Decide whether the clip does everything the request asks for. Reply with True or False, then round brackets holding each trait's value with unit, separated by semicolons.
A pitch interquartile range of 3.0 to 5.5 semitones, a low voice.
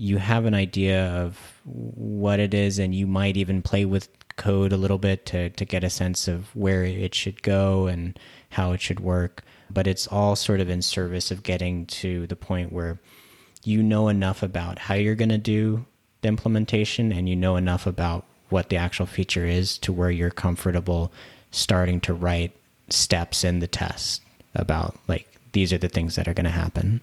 False (2.4 semitones; 95 Hz)